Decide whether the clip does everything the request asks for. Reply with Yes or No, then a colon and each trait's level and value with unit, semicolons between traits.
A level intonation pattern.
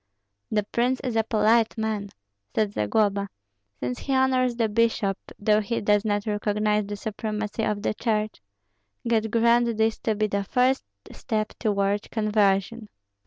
Yes: narrow, 1.9 semitones